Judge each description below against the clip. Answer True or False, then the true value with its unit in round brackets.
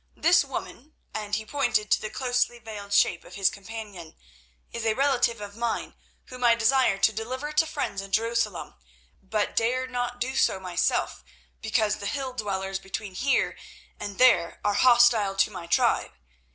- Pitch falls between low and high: False (220 Hz)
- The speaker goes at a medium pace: True (165 wpm)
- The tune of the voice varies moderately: True (3.9 semitones)